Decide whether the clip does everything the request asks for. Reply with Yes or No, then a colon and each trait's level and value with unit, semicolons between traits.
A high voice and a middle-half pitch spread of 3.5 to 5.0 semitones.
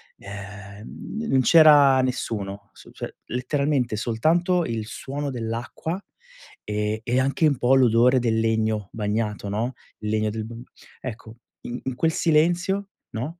No: low, 120 Hz; average, 4.6 semitones